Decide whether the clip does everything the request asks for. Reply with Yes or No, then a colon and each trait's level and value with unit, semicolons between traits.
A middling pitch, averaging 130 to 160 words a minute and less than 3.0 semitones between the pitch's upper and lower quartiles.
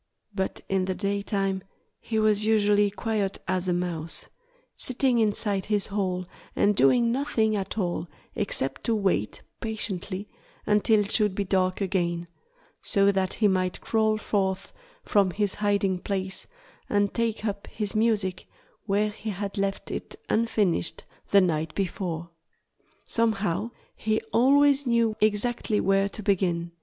No: high, 200 Hz; average, 140 wpm; narrow, 2.5 semitones